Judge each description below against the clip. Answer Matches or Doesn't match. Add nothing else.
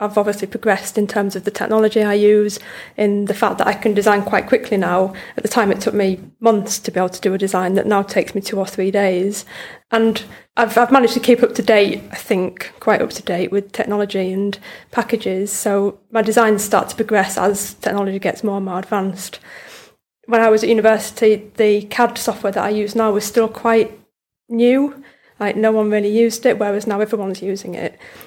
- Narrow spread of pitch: Matches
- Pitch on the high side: Matches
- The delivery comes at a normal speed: Doesn't match